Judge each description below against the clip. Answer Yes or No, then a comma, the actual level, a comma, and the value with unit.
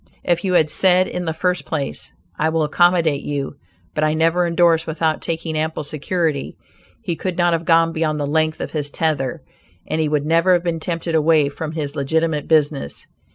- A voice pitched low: No, medium, 160 Hz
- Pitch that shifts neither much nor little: No, narrow, 1.8 semitones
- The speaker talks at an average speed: Yes, average, 195 wpm